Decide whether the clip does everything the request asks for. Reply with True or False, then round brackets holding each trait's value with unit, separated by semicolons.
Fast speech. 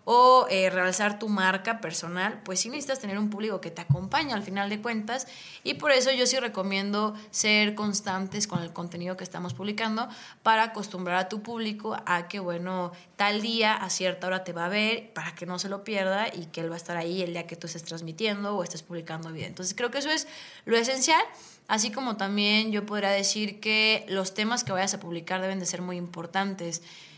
True (220 wpm)